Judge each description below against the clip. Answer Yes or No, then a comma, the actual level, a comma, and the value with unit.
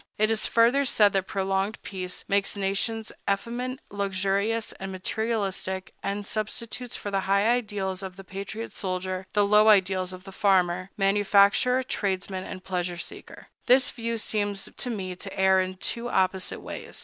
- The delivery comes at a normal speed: Yes, average, 160 wpm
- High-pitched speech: Yes, high, 200 Hz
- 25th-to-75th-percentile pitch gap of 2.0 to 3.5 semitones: Yes, narrow, 2.5 semitones